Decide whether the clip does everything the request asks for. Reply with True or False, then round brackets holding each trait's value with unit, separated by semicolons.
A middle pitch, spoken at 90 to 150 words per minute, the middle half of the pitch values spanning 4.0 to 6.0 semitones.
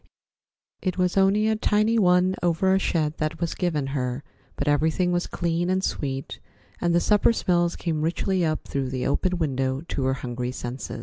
False (170 Hz; 185 wpm; 4.8 semitones)